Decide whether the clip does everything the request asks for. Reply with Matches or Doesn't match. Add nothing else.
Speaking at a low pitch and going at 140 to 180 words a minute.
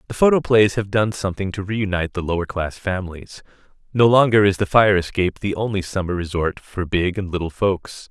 Doesn't match